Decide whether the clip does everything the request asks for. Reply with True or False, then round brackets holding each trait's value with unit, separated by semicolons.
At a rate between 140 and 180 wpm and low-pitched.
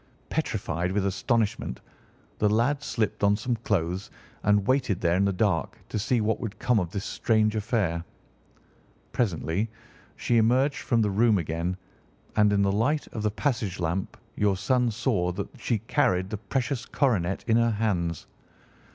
True (160 wpm; 105 Hz)